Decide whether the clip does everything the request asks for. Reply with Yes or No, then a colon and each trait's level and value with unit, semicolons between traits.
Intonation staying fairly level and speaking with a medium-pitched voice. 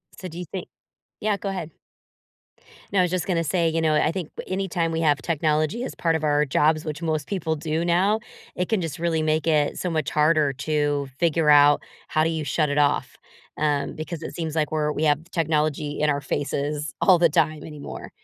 Yes: narrow, 2.1 semitones; medium, 155 Hz